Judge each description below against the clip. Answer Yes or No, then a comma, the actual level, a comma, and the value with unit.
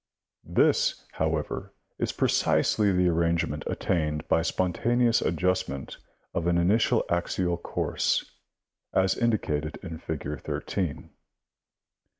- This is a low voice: Yes, very low, 85 Hz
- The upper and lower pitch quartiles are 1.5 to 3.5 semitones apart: Yes, average, 2.9 semitones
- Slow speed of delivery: Yes, slow, 105 wpm